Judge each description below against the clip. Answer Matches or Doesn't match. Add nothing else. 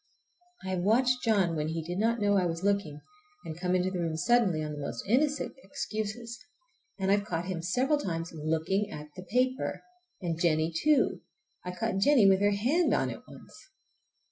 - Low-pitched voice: Doesn't match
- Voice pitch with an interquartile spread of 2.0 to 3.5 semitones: Doesn't match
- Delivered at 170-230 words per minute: Matches